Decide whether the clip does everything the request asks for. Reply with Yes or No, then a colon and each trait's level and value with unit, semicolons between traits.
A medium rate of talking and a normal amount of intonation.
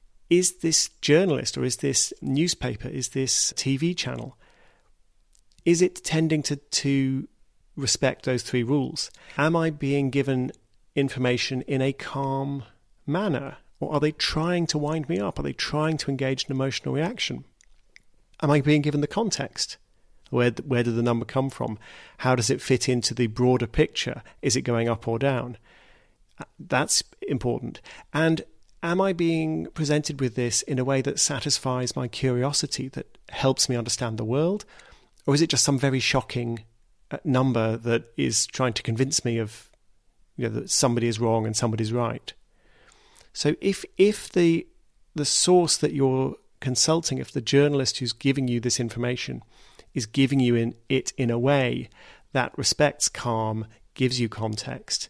Yes: average, 165 wpm; average, 3.5 semitones